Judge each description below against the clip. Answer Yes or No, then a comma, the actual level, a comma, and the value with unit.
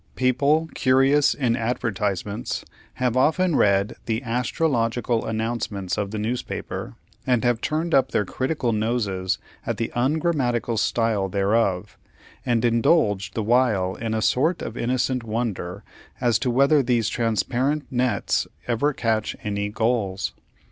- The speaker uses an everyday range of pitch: Yes, average, 3.2 semitones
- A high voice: No, low, 120 Hz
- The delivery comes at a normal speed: No, slow, 130 wpm